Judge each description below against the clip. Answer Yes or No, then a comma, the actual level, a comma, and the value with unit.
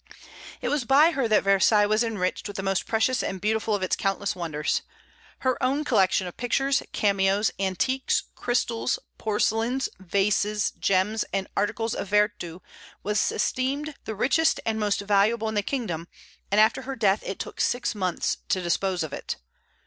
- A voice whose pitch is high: Yes, high, 210 Hz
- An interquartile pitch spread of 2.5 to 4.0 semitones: Yes, average, 3.4 semitones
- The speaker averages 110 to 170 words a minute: Yes, average, 165 wpm